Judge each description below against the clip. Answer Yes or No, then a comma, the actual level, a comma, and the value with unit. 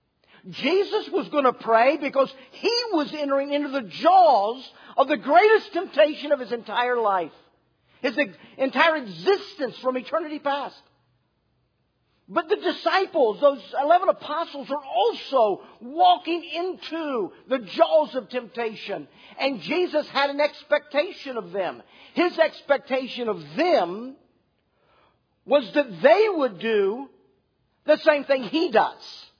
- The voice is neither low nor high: No, very high, 285 Hz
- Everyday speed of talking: No, slow, 125 wpm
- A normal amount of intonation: Yes, average, 5.0 semitones